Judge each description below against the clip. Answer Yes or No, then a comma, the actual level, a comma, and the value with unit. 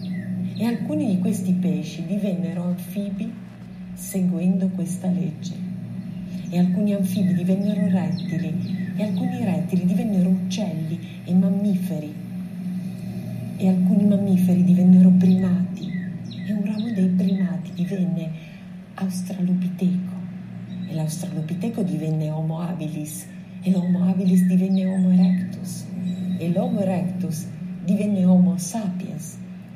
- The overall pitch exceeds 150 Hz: Yes, medium, 185 Hz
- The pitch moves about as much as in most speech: No, narrow, 0.8 semitones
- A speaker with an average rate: No, slow, 105 wpm